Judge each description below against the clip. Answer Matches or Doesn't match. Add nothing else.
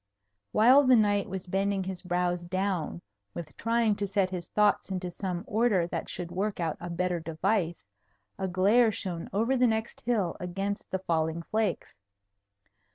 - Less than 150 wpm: Doesn't match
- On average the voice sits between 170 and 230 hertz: Matches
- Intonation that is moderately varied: Matches